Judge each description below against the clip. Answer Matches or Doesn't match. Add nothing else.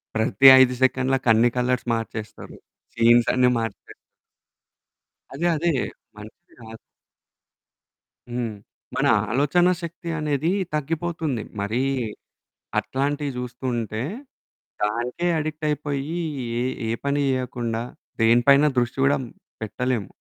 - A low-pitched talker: Matches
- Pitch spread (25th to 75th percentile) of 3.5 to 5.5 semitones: Matches